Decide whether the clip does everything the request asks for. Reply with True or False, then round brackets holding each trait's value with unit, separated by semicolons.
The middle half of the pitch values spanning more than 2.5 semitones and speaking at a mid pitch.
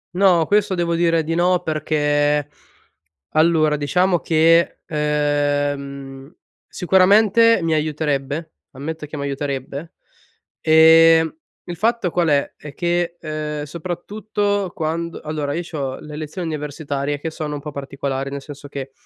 True (2.9 semitones; 155 Hz)